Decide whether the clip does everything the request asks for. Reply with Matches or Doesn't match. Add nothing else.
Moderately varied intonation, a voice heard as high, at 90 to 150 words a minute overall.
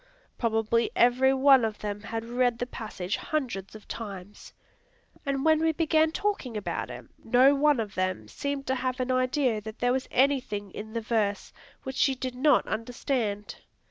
Doesn't match